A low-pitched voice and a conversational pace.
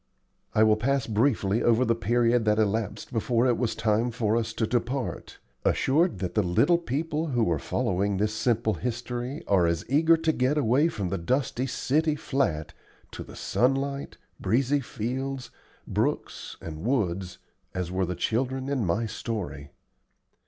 Yes: low, 115 Hz; average, 160 wpm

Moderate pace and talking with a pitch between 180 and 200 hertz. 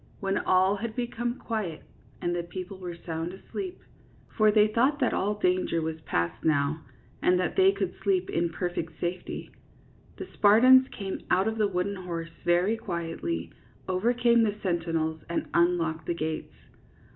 Yes: average, 170 wpm; medium, 185 Hz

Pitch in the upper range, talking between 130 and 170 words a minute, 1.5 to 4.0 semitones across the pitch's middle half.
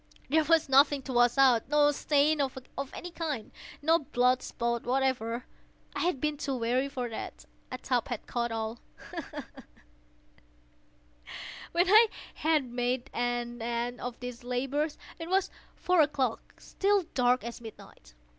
Yes: very high, 255 Hz; slow, 135 wpm; average, 3.6 semitones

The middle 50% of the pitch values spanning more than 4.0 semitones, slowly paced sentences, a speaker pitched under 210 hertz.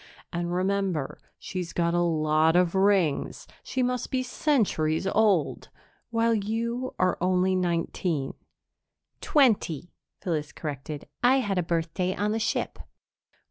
Yes: average, 4.7 semitones; slow, 125 wpm; medium, 185 Hz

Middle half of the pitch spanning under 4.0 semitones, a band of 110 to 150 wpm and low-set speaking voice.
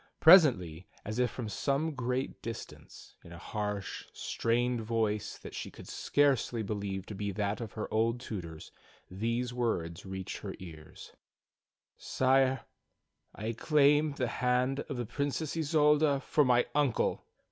No: average, 5.0 semitones; average, 140 wpm; low, 120 Hz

